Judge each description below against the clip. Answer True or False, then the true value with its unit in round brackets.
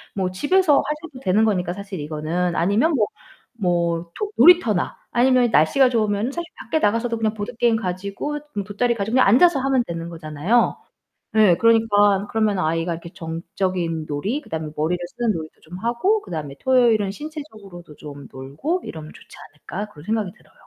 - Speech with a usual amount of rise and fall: False (6.0 semitones)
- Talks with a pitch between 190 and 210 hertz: True (205 Hz)